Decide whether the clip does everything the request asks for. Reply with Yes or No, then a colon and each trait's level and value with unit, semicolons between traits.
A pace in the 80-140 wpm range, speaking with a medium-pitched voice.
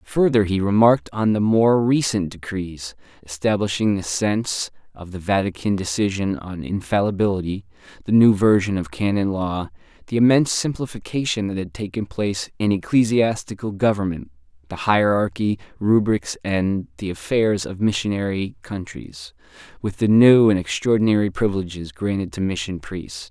No: slow, 135 wpm; low, 100 Hz